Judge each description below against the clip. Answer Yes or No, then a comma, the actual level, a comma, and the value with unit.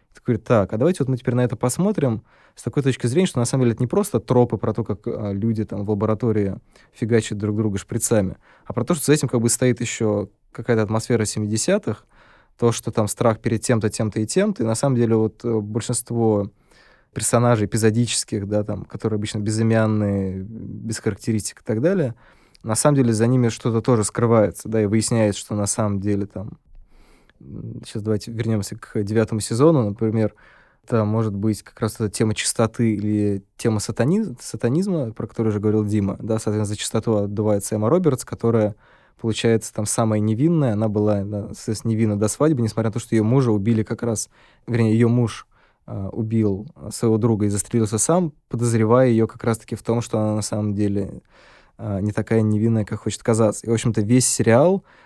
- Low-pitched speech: Yes, low, 110 Hz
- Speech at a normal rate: No, fast, 185 wpm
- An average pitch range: No, narrow, 2.0 semitones